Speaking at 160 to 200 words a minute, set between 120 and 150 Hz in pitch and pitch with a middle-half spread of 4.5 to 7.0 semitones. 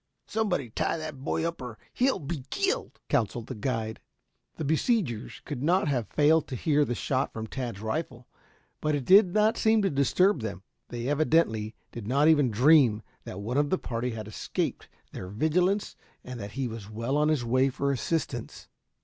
Yes: average, 185 wpm; low, 135 Hz; wide, 5.6 semitones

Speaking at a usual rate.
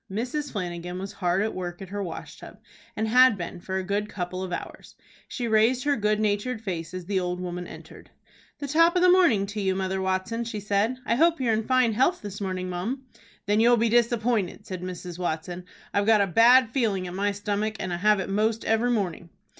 No: fast, 215 wpm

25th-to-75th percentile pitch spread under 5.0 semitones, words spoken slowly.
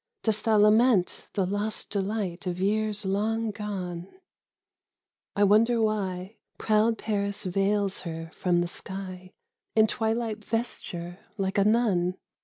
Yes: average, 2.8 semitones; slow, 125 wpm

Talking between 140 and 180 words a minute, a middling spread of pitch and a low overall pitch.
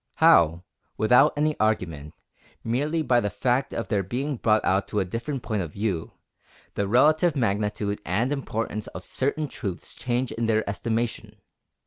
Yes: average, 155 wpm; average, 4.6 semitones; low, 110 Hz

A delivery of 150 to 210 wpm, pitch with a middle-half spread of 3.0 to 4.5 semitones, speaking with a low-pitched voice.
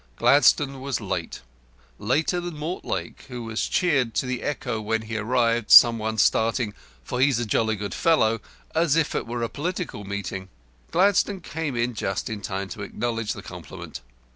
No: average, 170 wpm; average, 5.0 semitones; low, 120 Hz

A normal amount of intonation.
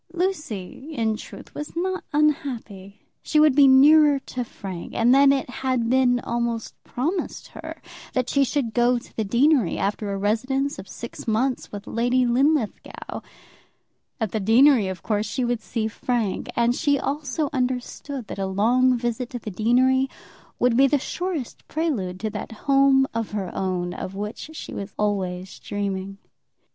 Yes: average, 4.6 semitones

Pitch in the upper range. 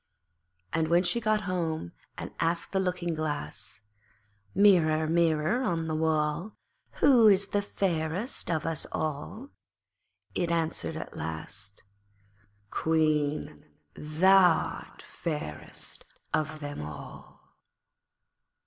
No: medium, 160 Hz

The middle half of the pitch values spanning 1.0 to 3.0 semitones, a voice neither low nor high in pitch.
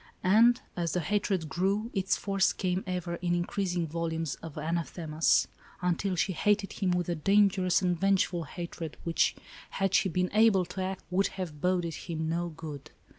Yes: narrow, 2.6 semitones; medium, 180 Hz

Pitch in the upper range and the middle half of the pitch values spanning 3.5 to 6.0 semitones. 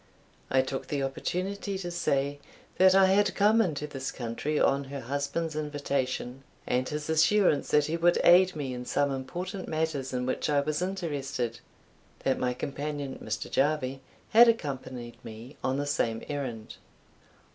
No: medium, 145 Hz; average, 4.4 semitones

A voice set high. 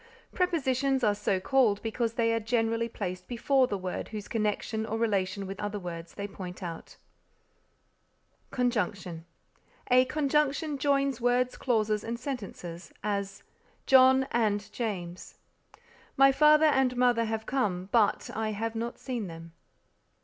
Yes: high, 225 Hz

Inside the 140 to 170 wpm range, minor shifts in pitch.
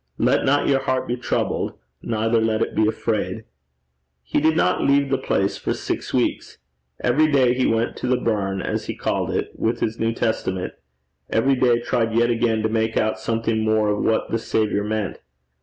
No: average, 190 wpm; narrow, 2.3 semitones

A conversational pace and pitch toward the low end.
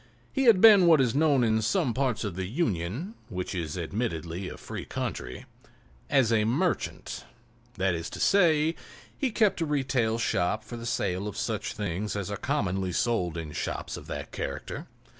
Yes: average, 180 wpm; low, 115 Hz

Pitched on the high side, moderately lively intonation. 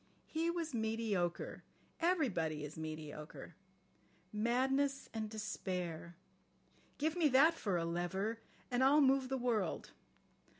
No: high, 220 Hz; wide, 7.7 semitones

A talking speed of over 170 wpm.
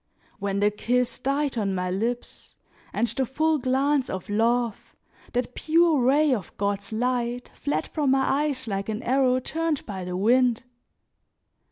No: average, 155 wpm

